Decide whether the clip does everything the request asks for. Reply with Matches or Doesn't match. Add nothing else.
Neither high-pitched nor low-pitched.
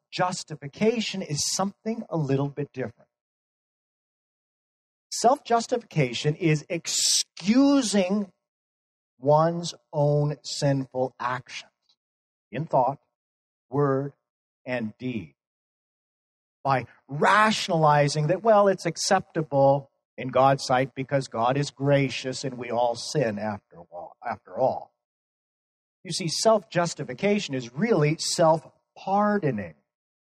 Matches